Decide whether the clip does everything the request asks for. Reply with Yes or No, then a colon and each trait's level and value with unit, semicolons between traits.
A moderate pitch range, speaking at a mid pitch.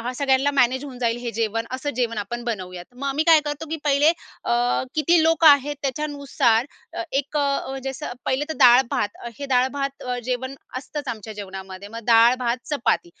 No: average, 3.6 semitones; very high, 260 Hz